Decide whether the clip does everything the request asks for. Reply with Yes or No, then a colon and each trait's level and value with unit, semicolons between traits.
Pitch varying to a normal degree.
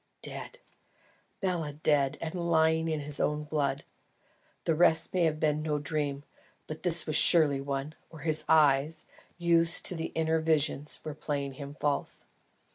No: narrow, 1.9 semitones